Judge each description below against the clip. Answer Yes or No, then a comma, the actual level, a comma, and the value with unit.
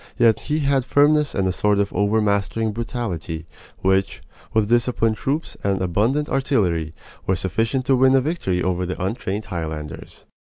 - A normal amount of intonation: No, wide, 5.7 semitones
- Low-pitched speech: Yes, low, 105 Hz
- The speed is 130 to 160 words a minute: Yes, average, 155 wpm